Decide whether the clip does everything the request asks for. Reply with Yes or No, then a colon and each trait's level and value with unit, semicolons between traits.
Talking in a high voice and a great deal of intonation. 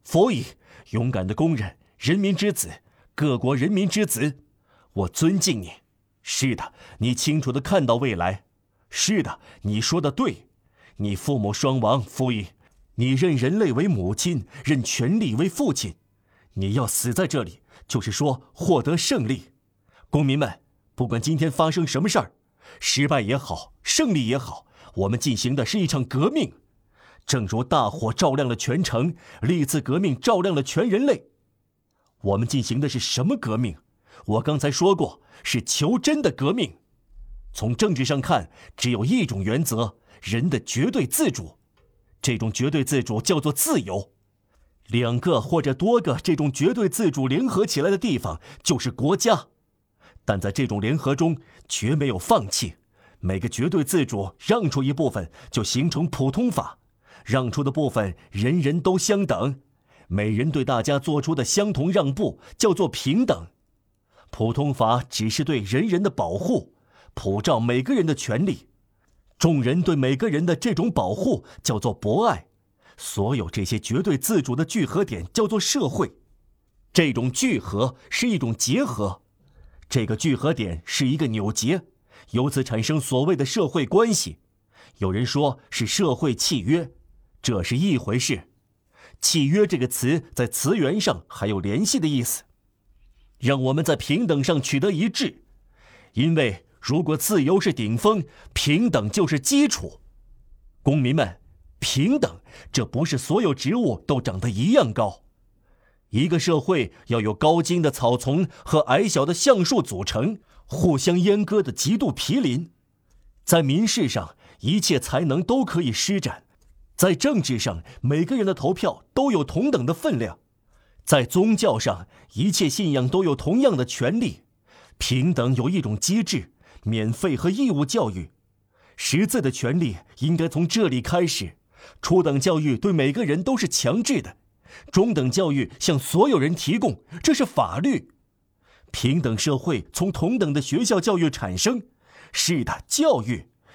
No: low, 135 Hz; wide, 7.5 semitones